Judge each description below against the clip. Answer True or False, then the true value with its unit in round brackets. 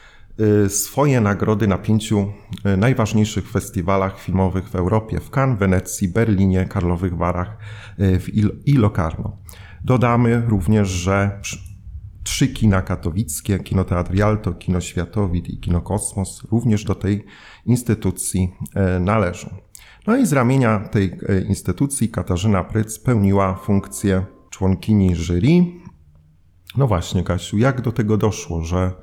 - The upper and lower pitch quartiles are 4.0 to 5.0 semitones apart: False (2.8 semitones)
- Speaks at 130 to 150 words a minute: False (115 wpm)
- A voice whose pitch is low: True (100 Hz)